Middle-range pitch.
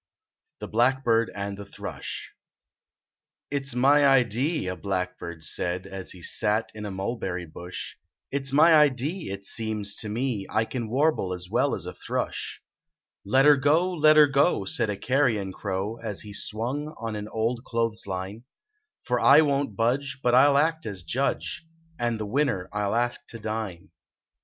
No: low, 115 Hz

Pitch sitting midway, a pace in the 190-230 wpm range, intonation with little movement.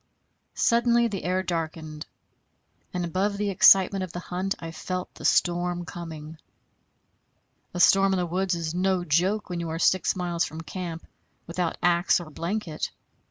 No: medium, 175 Hz; average, 160 wpm; narrow, 2.2 semitones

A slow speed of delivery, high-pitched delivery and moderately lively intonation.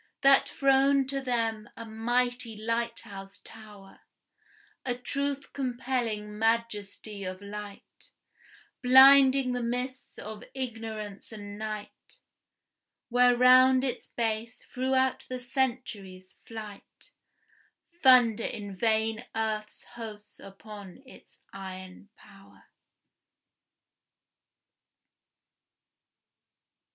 Yes: slow, 85 wpm; high, 230 Hz; average, 3.4 semitones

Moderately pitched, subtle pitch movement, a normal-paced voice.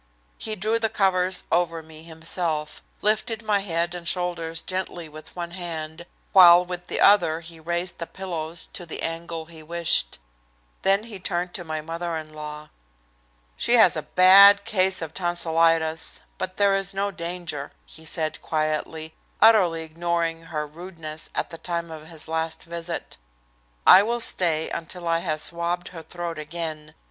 Yes: medium, 170 Hz; narrow, 2.2 semitones; average, 160 wpm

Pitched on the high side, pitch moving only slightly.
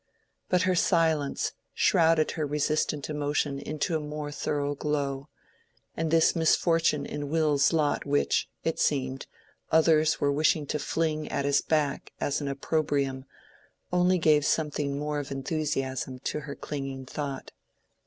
No: medium, 150 Hz; narrow, 1.9 semitones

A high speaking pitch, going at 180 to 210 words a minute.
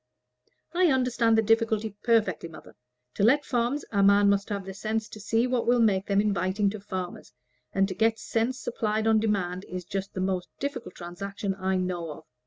Yes: high, 205 Hz; average, 195 wpm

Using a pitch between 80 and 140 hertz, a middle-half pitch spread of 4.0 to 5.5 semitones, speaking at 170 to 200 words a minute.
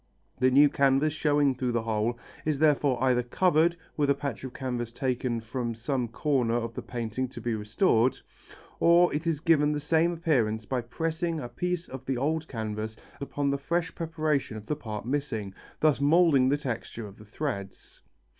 Yes: low, 135 Hz; average, 4.5 semitones; average, 185 wpm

